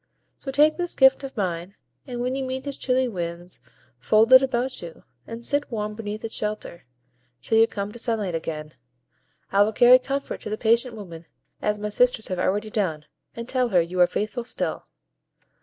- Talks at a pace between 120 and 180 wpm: No, average, 190 wpm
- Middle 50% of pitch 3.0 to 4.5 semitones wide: No, average, 5.1 semitones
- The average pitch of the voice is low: No, high, 220 Hz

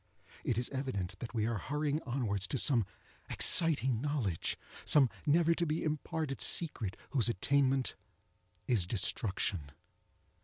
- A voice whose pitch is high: No, low, 130 Hz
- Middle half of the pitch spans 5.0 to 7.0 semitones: Yes, wide, 5.4 semitones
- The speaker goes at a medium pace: No, slow, 120 wpm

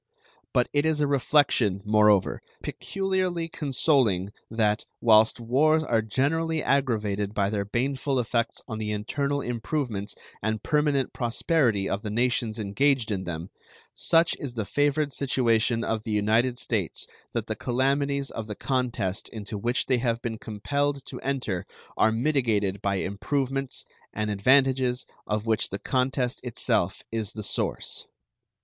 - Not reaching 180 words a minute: Yes, average, 140 wpm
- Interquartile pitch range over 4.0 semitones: Yes, average, 4.6 semitones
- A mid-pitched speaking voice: No, low, 120 Hz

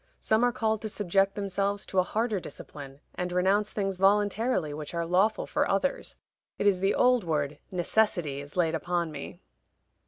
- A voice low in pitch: No, high, 195 Hz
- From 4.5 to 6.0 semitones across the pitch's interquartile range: No, average, 3.8 semitones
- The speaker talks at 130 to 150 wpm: No, average, 175 wpm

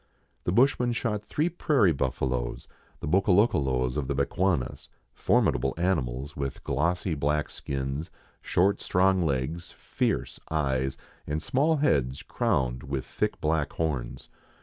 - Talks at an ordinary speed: No, slow, 125 wpm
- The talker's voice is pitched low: Yes, very low, 75 Hz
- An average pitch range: No, wide, 6.0 semitones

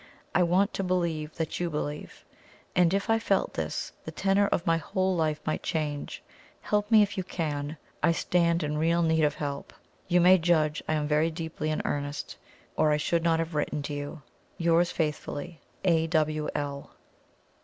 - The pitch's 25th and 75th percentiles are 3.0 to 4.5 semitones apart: No, narrow, 2.6 semitones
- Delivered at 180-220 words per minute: Yes, average, 185 wpm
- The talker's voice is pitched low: No, medium, 160 Hz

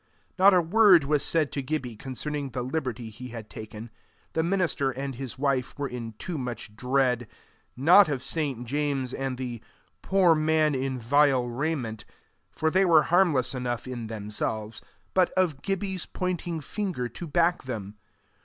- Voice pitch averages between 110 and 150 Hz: Yes, low, 135 Hz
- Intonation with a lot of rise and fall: No, average, 4.8 semitones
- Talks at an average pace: Yes, average, 160 wpm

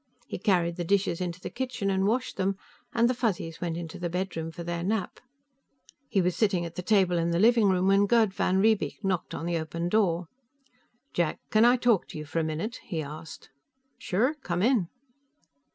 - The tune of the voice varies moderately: Yes, average, 4.1 semitones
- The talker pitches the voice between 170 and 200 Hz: Yes, medium, 185 Hz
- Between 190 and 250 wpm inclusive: Yes, average, 200 wpm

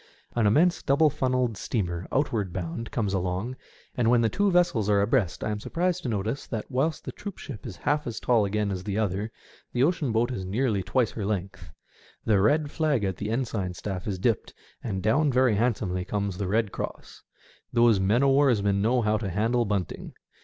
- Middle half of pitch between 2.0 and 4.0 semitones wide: No, average, 4.4 semitones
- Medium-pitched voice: No, low, 110 Hz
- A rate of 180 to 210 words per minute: Yes, average, 195 wpm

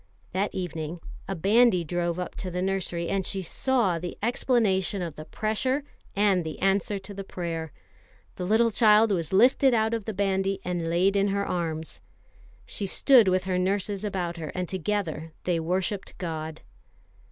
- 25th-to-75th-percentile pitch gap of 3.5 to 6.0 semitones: No, average, 3.0 semitones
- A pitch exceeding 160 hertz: Yes, high, 190 Hz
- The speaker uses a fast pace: No, average, 170 wpm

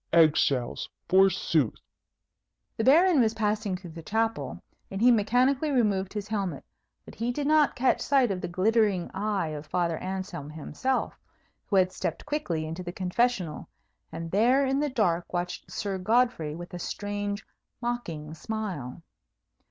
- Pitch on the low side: No, high, 200 Hz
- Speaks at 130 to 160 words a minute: Yes, average, 150 wpm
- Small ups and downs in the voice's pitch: No, wide, 5.4 semitones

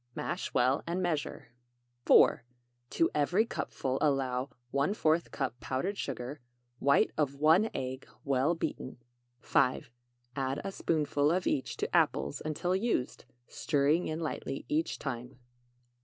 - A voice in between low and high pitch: Yes, medium, 145 Hz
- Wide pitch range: No, average, 4.1 semitones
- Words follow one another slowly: Yes, slow, 125 wpm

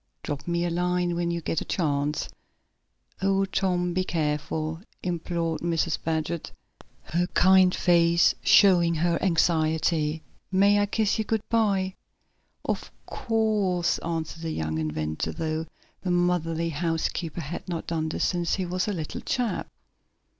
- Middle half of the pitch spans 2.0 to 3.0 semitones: Yes, narrow, 2.4 semitones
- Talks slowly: No, average, 145 wpm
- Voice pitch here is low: No, medium, 170 Hz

